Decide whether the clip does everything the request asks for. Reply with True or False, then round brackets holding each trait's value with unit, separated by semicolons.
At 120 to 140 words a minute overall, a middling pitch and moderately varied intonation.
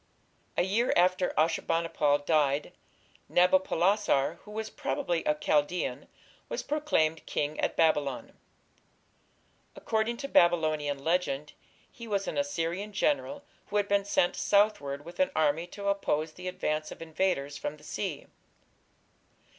True (135 wpm; 175 Hz; 4.9 semitones)